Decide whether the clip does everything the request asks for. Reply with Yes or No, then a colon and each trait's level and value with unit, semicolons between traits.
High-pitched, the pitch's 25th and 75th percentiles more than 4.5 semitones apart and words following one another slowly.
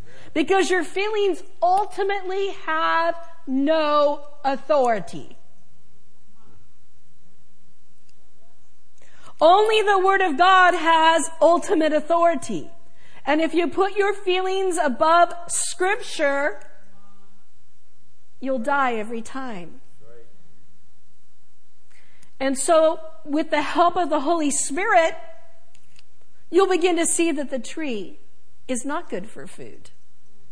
Yes: very high, 325 Hz; average, 4.9 semitones; slow, 95 wpm